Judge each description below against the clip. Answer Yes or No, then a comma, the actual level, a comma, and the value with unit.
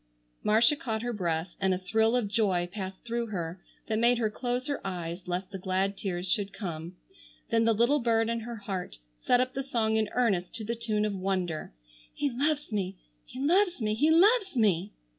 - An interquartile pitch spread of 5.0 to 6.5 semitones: No, average, 4.2 semitones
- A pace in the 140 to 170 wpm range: No, average, 200 wpm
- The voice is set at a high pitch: Yes, high, 215 Hz